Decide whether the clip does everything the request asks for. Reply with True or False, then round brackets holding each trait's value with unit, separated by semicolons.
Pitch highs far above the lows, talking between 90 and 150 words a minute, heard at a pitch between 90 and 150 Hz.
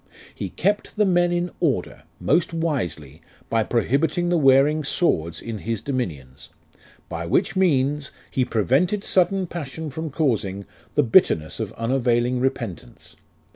True (7.1 semitones; 135 wpm; 135 Hz)